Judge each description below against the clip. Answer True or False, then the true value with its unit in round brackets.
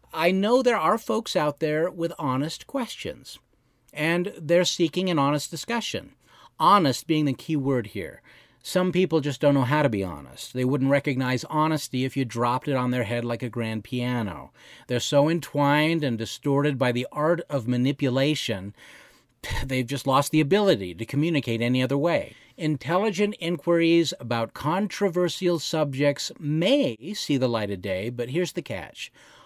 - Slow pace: False (165 wpm)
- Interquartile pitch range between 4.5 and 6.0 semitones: True (5.1 semitones)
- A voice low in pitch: False (145 Hz)